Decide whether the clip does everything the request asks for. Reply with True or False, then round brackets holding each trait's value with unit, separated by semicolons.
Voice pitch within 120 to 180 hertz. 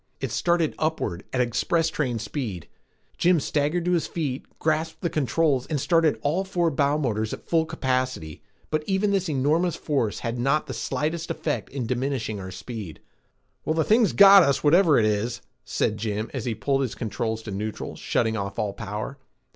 True (140 Hz)